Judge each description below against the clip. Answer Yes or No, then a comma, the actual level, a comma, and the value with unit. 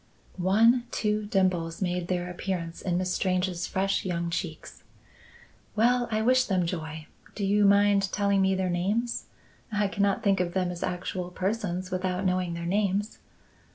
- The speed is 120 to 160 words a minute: Yes, average, 155 wpm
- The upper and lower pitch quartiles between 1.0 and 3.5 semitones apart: Yes, narrow, 2.4 semitones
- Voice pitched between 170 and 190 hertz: Yes, medium, 185 Hz